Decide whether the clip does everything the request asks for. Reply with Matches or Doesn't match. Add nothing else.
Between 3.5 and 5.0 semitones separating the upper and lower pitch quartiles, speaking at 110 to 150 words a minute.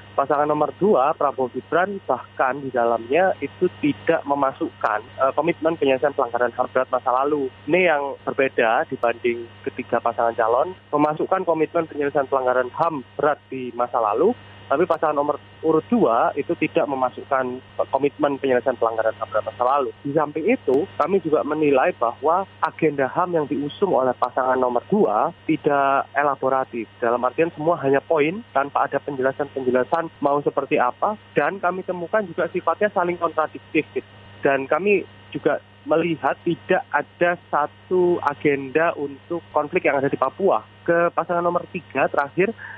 Matches